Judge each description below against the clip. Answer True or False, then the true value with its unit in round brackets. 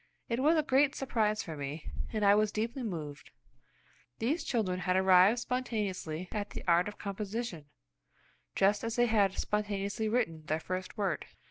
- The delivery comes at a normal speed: True (160 wpm)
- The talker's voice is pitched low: False (205 Hz)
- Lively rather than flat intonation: False (4.0 semitones)